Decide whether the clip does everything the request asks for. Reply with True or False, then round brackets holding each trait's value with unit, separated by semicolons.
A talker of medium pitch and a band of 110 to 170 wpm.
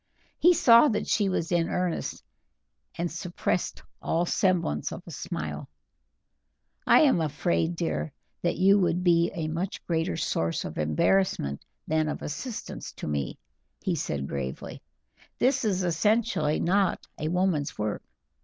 True (170 Hz; 140 wpm)